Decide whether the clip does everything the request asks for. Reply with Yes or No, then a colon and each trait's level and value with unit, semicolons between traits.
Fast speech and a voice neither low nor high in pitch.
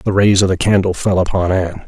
No: fast, 255 wpm; very low, 95 Hz